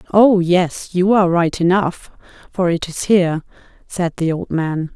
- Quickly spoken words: No, average, 170 wpm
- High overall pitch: No, medium, 175 Hz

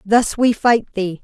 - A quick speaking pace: No, average, 195 wpm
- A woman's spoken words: Yes, female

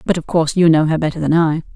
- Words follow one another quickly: Yes, fast, 310 wpm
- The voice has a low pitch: No, medium, 160 Hz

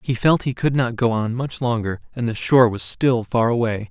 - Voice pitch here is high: No, low, 120 Hz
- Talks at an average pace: No, fast, 245 wpm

